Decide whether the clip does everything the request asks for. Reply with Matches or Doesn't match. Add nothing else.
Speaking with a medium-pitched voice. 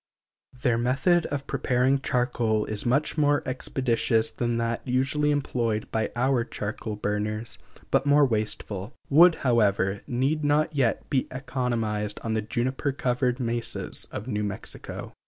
Doesn't match